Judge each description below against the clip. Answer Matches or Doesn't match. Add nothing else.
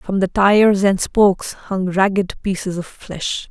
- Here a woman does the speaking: Matches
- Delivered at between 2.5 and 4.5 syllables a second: Matches